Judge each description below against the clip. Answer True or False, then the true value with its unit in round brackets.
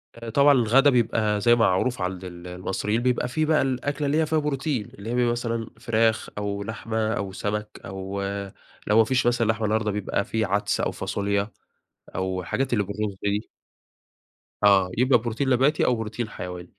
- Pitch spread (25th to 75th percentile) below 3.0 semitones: False (3.3 semitones)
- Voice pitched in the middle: False (110 Hz)